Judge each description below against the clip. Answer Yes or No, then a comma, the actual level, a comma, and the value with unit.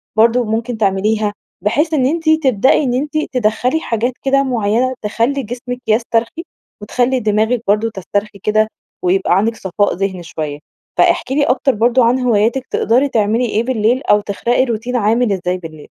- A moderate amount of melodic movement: Yes, average, 3.3 semitones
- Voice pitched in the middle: No, high, 225 Hz